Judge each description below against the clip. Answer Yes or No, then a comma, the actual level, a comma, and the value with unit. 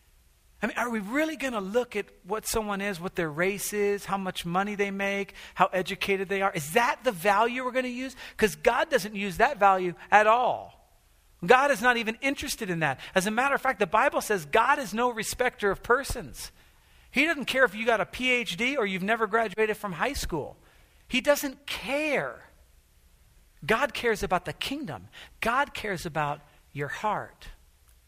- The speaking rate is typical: Yes, average, 190 wpm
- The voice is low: No, high, 210 Hz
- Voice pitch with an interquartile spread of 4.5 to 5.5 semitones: Yes, average, 5.1 semitones